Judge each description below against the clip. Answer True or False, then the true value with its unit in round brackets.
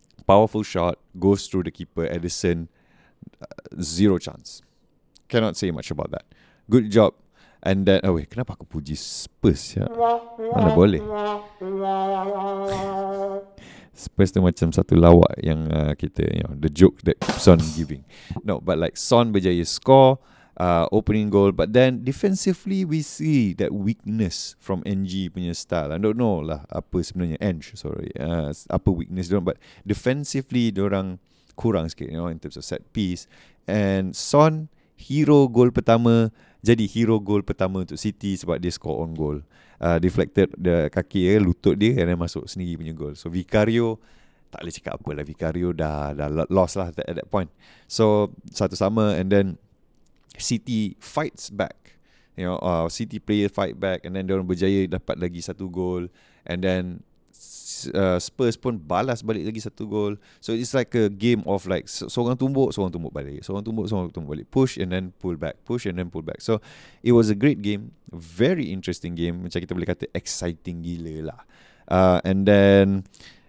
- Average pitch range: True (4.6 semitones)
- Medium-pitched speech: False (95 Hz)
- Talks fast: True (175 wpm)